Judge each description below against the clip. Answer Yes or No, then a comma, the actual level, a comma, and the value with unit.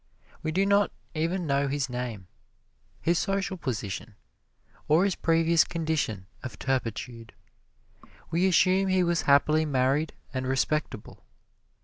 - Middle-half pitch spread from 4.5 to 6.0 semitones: Yes, average, 5.0 semitones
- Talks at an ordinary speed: No, slow, 120 wpm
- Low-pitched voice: No, medium, 155 Hz